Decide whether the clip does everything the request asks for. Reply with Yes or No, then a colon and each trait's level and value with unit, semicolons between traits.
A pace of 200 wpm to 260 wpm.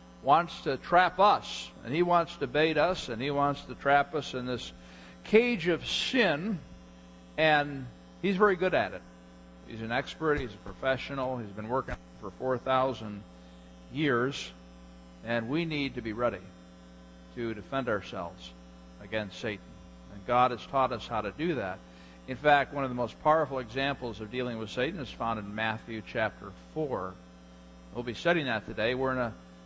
No: average, 170 wpm